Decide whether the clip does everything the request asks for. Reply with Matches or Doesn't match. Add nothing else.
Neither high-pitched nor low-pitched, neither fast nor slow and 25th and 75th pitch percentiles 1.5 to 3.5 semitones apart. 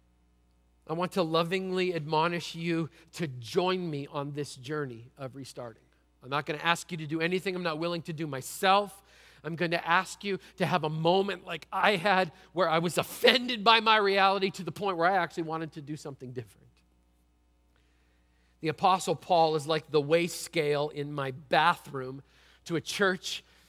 Doesn't match